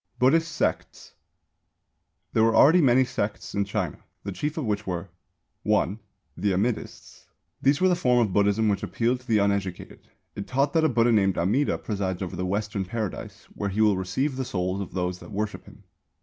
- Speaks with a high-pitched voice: No, low, 105 Hz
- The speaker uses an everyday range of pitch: Yes, average, 4.6 semitones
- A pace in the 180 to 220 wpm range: Yes, average, 190 wpm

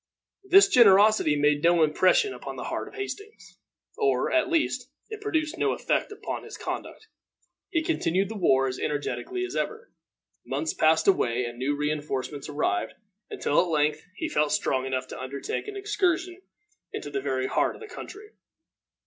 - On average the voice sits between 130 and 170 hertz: No, medium, 185 Hz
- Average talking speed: Yes, average, 170 wpm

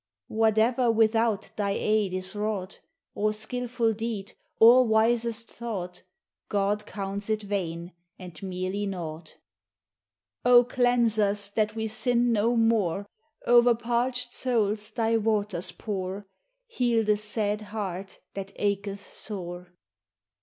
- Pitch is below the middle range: No, high, 215 Hz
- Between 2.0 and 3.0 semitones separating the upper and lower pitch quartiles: Yes, narrow, 2.6 semitones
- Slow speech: Yes, slow, 120 wpm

